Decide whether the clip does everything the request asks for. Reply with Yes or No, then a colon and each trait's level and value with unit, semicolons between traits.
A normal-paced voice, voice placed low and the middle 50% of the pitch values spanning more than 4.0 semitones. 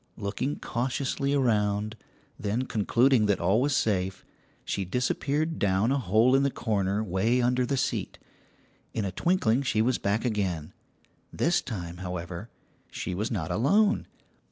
Yes: average, 145 wpm; low, 110 Hz; average, 4.7 semitones